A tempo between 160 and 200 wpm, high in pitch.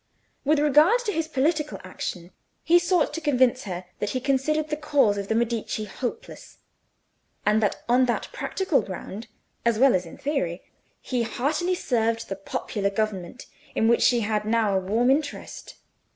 Yes: average, 165 wpm; high, 245 Hz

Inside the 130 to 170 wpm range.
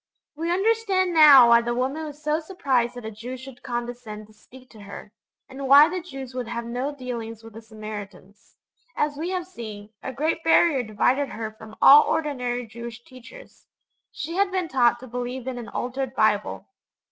No: average, 185 wpm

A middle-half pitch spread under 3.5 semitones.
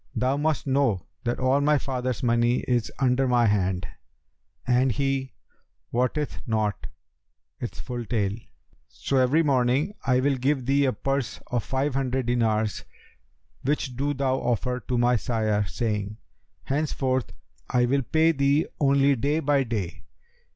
Yes: average, 2.7 semitones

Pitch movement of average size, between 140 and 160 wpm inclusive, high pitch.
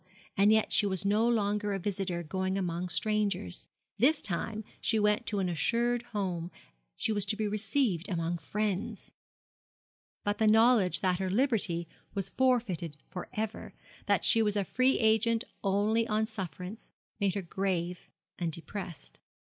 Yes: average, 3.3 semitones; average, 155 wpm; high, 205 Hz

